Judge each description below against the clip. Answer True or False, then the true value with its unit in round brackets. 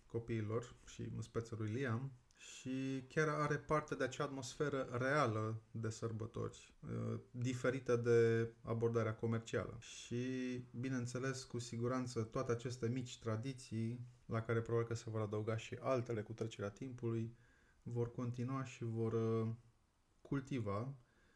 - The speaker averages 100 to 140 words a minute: True (125 wpm)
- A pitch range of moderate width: False (2.1 semitones)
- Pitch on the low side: True (120 Hz)